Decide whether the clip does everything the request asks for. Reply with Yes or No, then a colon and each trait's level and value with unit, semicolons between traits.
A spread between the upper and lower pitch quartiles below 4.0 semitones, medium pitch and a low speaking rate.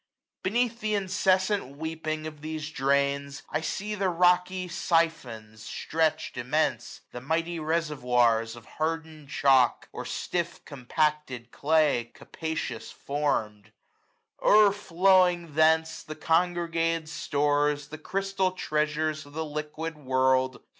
Yes: average, 3.4 semitones; medium, 155 Hz; slow, 120 wpm